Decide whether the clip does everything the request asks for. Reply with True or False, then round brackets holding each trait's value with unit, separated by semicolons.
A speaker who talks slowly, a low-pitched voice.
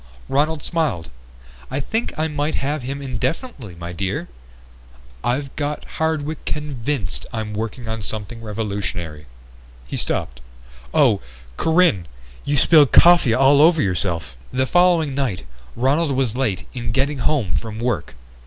True (130 wpm; 130 Hz)